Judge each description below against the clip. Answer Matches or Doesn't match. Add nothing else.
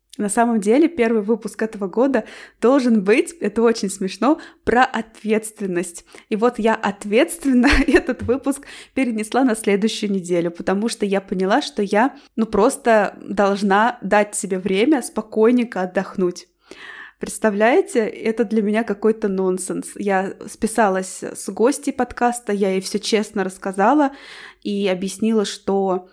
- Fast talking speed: Doesn't match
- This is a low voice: Doesn't match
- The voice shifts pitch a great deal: Doesn't match